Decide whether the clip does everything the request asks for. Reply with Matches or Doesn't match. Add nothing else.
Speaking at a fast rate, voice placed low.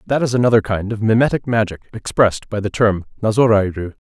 Doesn't match